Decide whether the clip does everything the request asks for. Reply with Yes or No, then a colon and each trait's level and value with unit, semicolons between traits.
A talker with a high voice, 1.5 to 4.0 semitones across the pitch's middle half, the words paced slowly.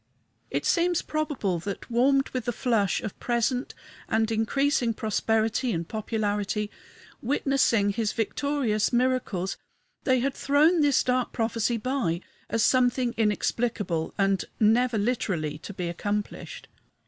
Yes: high, 230 Hz; average, 3.7 semitones; slow, 125 wpm